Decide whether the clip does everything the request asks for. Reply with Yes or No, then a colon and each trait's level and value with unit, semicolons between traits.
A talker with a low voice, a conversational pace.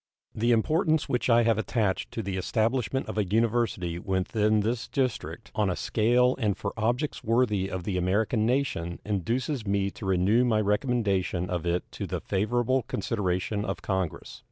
Yes: low, 110 Hz; average, 165 wpm